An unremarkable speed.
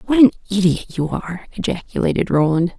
Yes: average, 150 wpm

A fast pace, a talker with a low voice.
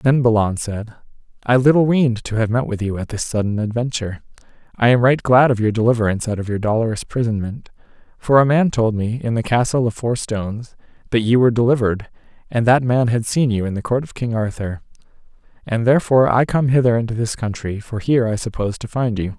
Yes: fast, 215 wpm; low, 115 Hz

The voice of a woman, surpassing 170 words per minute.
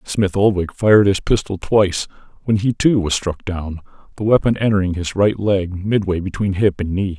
No: male; average, 190 wpm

